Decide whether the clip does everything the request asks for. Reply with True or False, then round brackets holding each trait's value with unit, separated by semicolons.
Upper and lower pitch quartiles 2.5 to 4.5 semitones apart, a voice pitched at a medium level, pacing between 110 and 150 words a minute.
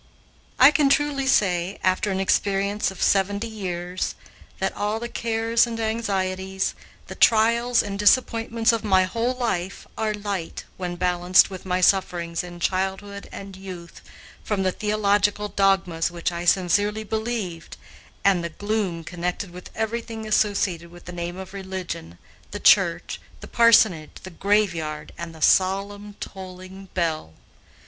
False (3.2 semitones; 195 Hz; 140 wpm)